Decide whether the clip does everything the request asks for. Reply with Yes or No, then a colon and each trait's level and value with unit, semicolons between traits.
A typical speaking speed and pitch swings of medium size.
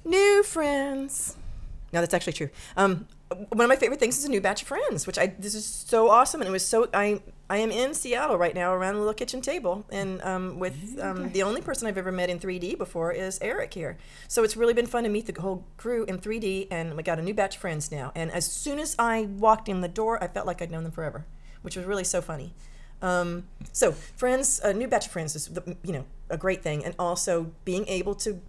No: fast, 245 wpm; average, 4.4 semitones